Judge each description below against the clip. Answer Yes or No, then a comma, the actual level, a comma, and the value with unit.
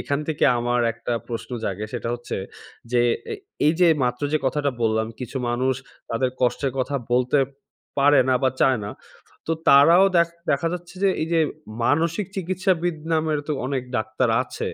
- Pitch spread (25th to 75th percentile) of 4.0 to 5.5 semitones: Yes, average, 5.0 semitones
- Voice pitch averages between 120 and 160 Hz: Yes, medium, 140 Hz